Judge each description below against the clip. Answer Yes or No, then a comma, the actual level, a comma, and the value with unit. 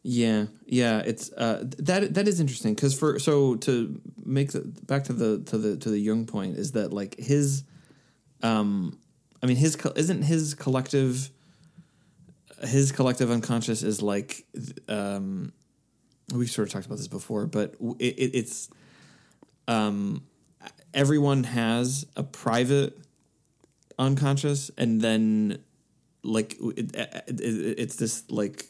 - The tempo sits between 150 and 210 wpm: No, average, 140 wpm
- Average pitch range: Yes, average, 4.3 semitones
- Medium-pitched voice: No, low, 125 Hz